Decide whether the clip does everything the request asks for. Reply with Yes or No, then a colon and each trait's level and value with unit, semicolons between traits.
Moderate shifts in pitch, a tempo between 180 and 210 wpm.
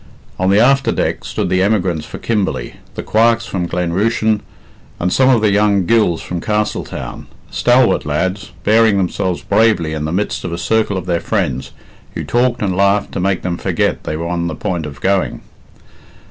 Yes: average, 3.9 semitones; average, 190 wpm